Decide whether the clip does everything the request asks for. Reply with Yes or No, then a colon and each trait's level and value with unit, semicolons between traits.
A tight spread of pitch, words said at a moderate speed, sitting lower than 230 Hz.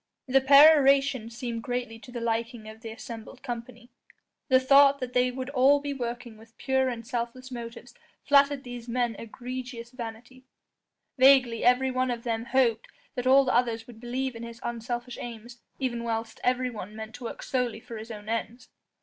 No: narrow, 2.0 semitones; average, 175 wpm; high, 245 Hz